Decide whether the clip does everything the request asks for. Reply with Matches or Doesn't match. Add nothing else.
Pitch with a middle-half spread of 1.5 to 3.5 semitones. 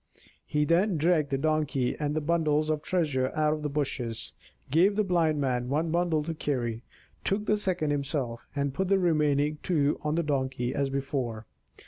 Matches